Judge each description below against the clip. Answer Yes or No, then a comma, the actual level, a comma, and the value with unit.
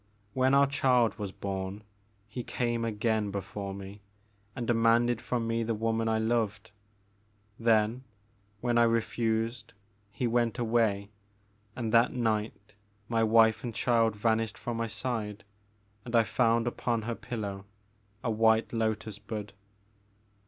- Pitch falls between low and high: No, low, 115 Hz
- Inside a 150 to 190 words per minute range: No, average, 140 wpm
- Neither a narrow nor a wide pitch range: No, narrow, 1.7 semitones